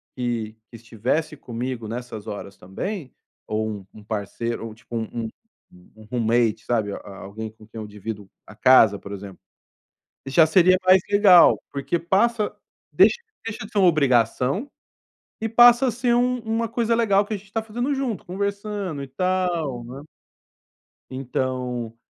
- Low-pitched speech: Yes, low, 130 Hz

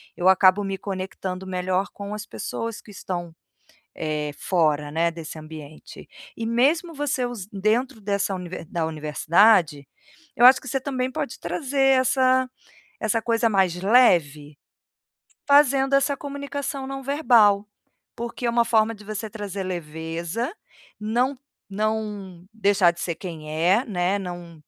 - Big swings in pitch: Yes, wide, 5.9 semitones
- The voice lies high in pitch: Yes, high, 205 Hz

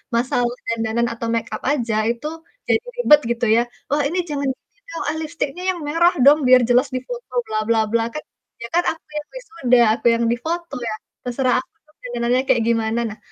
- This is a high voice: Yes, very high, 250 Hz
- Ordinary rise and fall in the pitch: Yes, average, 4.3 semitones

